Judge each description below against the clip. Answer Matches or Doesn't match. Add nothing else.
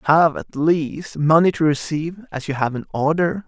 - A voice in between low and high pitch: Matches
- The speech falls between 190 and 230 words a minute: Matches